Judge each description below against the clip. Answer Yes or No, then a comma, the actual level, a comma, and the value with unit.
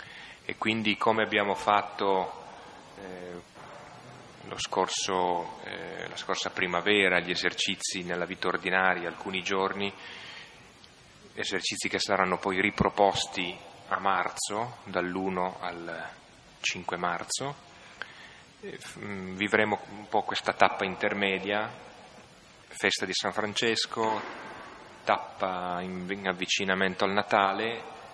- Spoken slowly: Yes, slow, 95 wpm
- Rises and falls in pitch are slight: Yes, narrow, 2.1 semitones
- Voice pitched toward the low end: Yes, very low, 95 Hz